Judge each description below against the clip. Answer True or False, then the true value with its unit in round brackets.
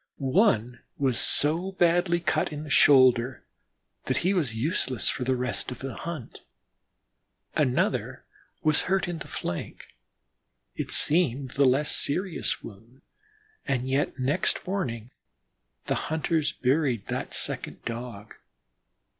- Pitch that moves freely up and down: False (4.8 semitones)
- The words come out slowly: True (125 wpm)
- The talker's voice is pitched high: False (140 Hz)